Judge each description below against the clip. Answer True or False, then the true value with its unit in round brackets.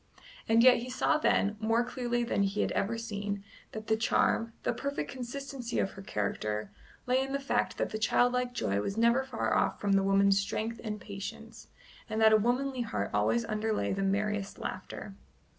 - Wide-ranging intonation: False (3.7 semitones)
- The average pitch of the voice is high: True (220 Hz)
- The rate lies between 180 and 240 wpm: True (190 wpm)